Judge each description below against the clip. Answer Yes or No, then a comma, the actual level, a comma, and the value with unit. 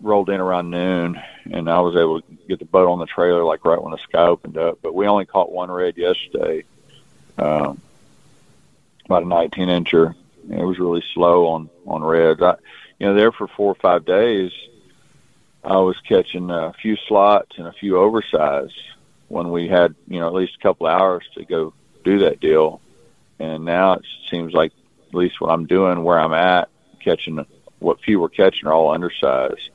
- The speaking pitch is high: No, very low, 90 Hz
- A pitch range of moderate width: No, narrow, 2.3 semitones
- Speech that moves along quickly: No, average, 195 wpm